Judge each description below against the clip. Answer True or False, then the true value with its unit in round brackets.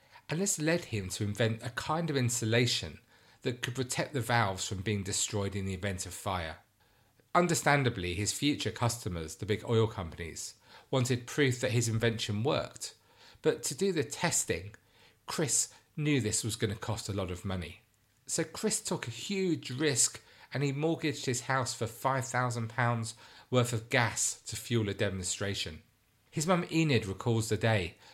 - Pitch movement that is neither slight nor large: True (4.4 semitones)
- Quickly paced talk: False (170 wpm)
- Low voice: True (115 Hz)